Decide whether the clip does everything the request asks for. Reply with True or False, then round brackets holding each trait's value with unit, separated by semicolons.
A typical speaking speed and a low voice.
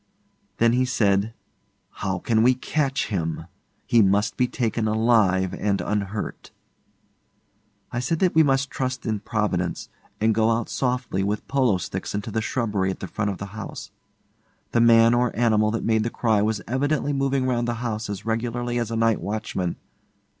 True (175 wpm; 115 Hz)